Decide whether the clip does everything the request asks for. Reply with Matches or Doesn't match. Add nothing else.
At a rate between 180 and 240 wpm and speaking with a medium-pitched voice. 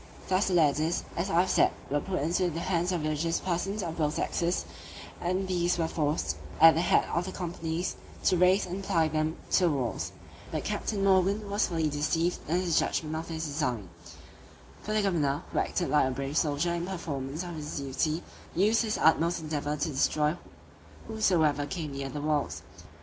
Matches